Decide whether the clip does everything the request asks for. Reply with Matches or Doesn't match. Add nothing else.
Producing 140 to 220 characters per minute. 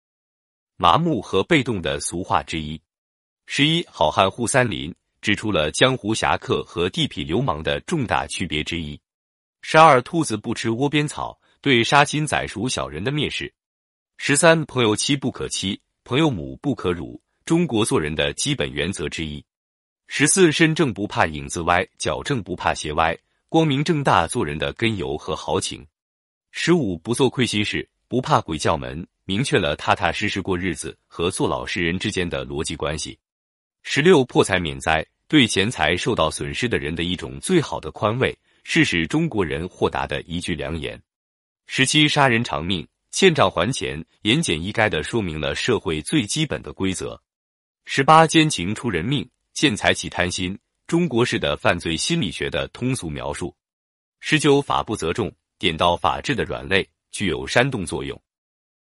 Doesn't match